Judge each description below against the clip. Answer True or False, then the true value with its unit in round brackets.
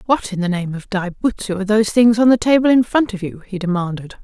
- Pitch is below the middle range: False (205 Hz)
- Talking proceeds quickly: True (270 wpm)